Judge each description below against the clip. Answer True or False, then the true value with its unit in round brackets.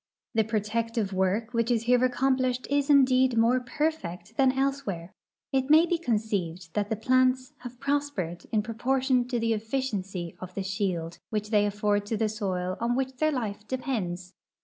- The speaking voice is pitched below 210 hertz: False (230 Hz)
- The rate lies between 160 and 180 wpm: True (175 wpm)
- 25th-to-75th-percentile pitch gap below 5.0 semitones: True (4.3 semitones)